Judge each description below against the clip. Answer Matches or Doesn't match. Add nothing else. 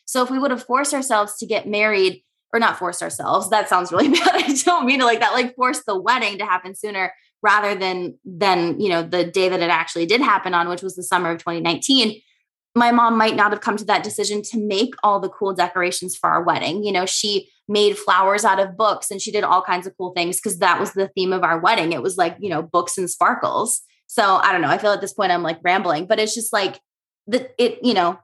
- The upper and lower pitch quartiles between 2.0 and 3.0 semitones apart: Doesn't match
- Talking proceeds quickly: Matches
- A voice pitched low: Doesn't match